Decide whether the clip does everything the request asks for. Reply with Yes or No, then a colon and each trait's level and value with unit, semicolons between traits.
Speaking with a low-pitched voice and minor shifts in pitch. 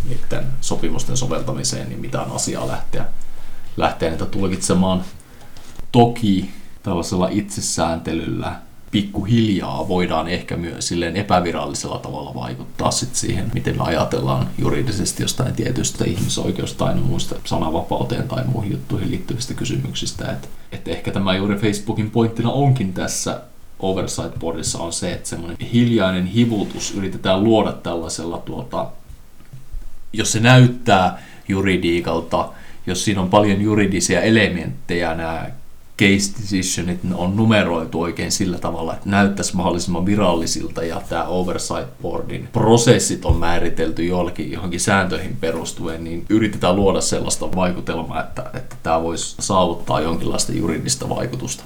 No: very low, 90 Hz; average, 4.0 semitones